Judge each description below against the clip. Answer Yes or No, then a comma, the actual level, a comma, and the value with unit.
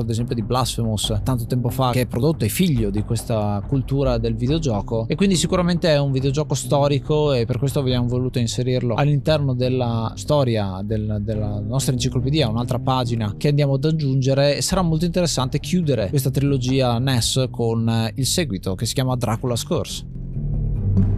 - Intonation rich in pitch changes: No, average, 3.5 semitones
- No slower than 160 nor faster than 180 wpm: Yes, average, 165 wpm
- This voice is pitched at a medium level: No, low, 130 Hz